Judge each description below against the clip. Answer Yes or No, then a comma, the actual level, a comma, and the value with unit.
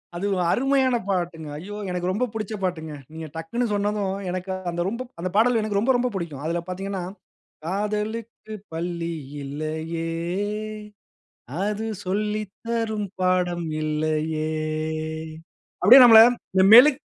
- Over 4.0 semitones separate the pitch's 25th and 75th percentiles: Yes, average, 4.5 semitones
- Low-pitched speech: No, high, 190 Hz